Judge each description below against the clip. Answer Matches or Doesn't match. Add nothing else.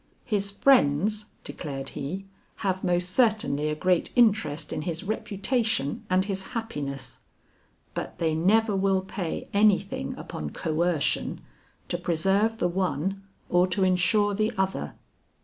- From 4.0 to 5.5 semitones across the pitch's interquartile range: Matches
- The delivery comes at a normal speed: Doesn't match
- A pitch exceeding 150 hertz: Matches